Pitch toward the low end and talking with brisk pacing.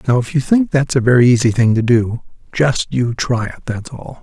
Yes: low, 125 Hz; fast, 240 wpm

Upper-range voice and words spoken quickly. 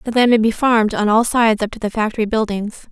Yes: high, 220 Hz; fast, 270 wpm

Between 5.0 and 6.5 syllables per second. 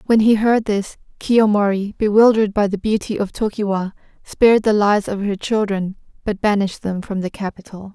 Yes: 5.4 syllables/s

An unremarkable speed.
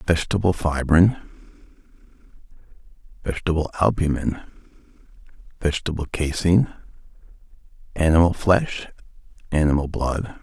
No: slow, 60 wpm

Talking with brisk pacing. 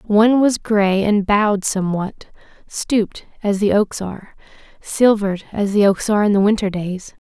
No: average, 165 wpm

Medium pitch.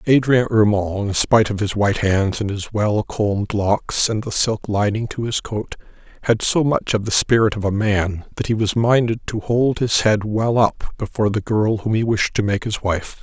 No: low, 105 Hz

